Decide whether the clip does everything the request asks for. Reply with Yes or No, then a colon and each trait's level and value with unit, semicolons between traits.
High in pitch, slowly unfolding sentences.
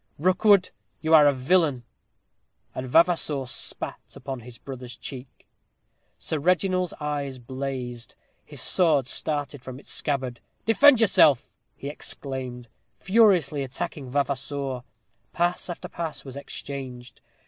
No: medium, 140 Hz; slow, 115 wpm